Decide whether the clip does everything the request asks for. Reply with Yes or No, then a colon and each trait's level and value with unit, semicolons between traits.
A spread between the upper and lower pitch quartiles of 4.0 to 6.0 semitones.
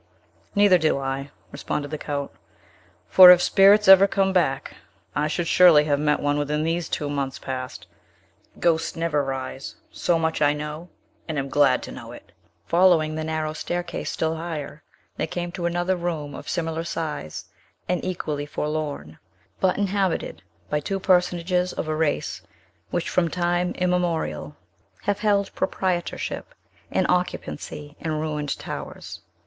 No: average, 3.3 semitones